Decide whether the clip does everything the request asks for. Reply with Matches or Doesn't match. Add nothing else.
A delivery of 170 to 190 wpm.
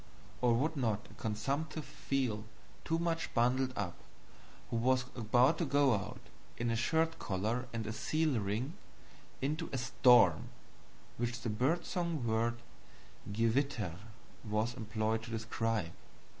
Doesn't match